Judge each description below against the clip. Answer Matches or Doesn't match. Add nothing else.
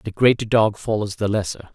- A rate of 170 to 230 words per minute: Matches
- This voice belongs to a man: Matches